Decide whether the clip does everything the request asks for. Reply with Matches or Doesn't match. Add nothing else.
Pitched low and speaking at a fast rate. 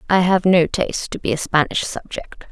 Doesn't match